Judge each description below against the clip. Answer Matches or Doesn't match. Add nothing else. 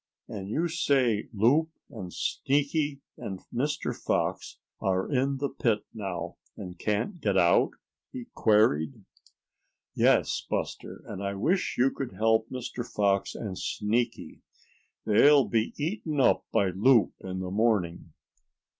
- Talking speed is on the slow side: Matches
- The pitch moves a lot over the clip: Matches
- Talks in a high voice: Doesn't match